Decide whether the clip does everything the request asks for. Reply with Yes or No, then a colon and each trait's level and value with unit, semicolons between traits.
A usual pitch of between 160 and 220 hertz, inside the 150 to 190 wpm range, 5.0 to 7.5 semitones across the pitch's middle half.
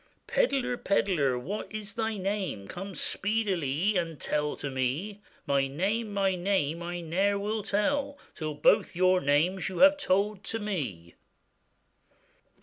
No: high, 190 Hz; average, 140 wpm; wide, 5.4 semitones